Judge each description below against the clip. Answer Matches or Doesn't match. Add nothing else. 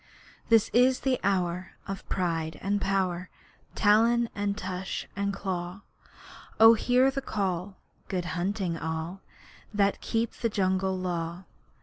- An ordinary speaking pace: Doesn't match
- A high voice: Matches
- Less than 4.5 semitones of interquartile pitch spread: Matches